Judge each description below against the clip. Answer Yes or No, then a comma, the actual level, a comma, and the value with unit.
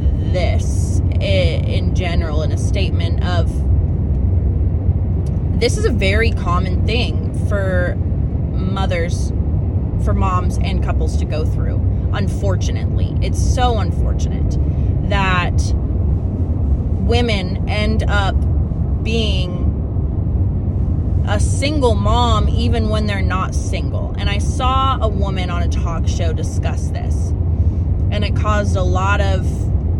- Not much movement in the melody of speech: Yes, narrow, 2.0 semitones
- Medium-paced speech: No, slow, 110 wpm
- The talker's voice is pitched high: No, very low, 90 Hz